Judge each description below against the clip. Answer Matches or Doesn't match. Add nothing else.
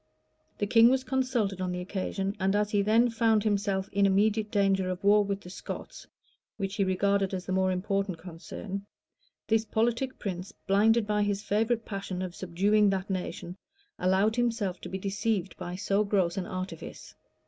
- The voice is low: Doesn't match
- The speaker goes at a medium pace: Matches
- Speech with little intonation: Matches